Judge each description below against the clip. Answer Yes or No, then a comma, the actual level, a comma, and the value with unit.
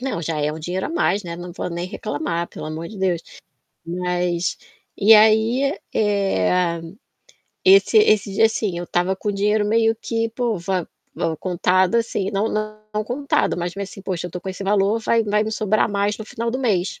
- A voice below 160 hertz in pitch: No, high, 200 Hz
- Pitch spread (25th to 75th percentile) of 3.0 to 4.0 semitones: Yes, average, 3.7 semitones